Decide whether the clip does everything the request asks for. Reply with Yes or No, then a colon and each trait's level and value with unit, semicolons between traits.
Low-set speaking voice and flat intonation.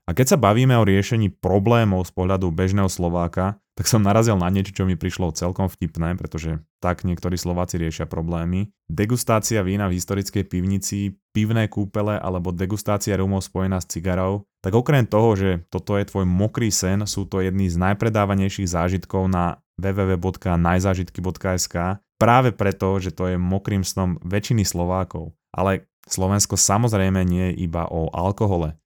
Yes: very low, 95 Hz; narrow, 2.0 semitones